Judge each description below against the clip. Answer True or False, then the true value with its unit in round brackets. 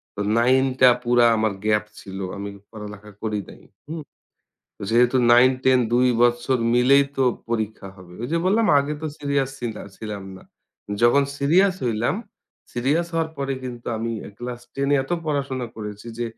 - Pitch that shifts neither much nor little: True (3.9 semitones)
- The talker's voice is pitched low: True (120 Hz)